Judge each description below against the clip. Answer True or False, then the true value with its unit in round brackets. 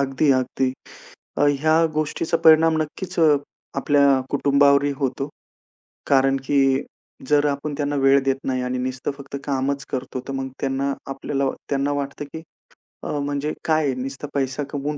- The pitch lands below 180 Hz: True (140 Hz)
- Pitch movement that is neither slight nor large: False (1.5 semitones)